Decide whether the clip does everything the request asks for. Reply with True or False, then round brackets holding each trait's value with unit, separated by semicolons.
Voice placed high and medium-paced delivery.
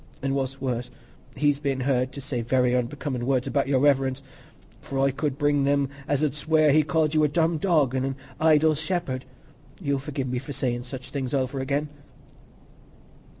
False (140 Hz; 190 wpm)